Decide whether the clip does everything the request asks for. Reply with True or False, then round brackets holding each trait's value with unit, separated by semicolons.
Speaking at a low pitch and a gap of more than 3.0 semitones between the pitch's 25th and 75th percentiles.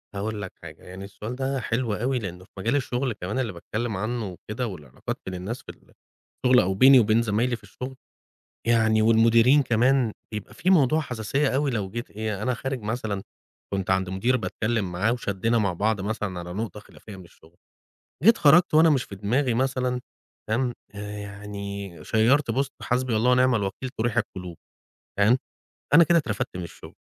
True (110 Hz; 4.1 semitones)